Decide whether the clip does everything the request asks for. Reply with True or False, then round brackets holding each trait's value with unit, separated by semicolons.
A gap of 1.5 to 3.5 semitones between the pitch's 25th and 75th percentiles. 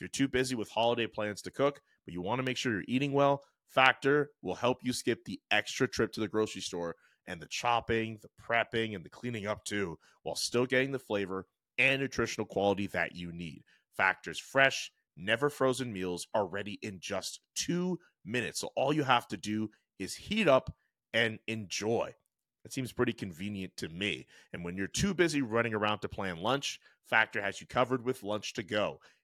False (4.3 semitones)